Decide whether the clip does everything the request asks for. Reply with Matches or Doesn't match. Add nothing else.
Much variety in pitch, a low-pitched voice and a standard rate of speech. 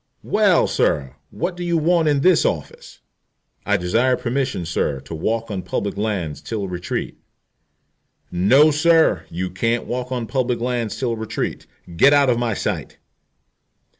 Matches